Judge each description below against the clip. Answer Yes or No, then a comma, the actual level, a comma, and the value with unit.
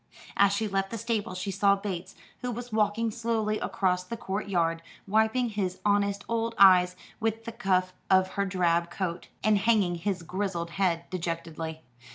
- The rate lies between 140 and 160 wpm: No, average, 170 wpm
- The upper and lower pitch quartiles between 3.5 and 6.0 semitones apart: No, average, 3.0 semitones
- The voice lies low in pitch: No, high, 195 Hz